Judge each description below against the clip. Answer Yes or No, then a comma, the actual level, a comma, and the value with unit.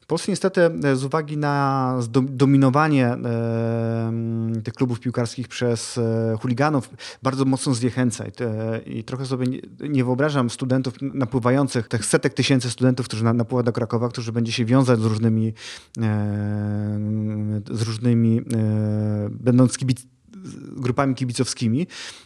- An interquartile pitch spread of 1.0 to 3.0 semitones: Yes, narrow, 2.6 semitones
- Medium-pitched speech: No, low, 125 Hz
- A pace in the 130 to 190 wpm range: No, average, 115 wpm